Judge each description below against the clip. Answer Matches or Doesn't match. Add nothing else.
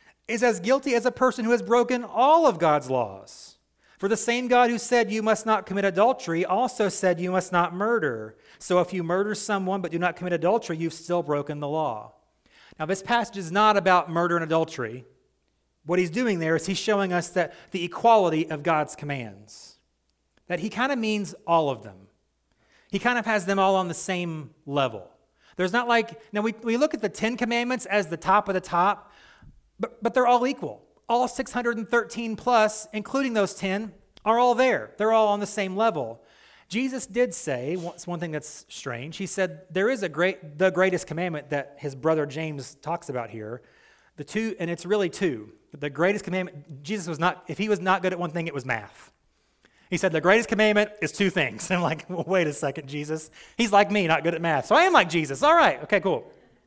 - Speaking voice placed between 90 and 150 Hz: Doesn't match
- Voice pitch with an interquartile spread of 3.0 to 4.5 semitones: Doesn't match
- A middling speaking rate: Doesn't match